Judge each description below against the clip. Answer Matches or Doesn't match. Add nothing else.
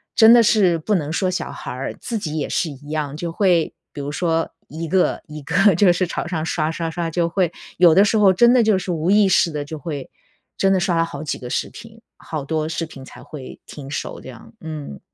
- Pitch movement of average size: Matches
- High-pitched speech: Doesn't match